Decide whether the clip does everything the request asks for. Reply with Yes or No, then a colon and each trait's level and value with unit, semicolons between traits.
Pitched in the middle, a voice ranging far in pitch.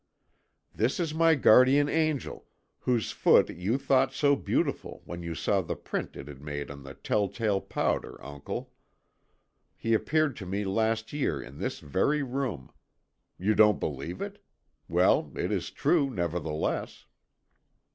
No: low, 110 Hz; wide, 8.5 semitones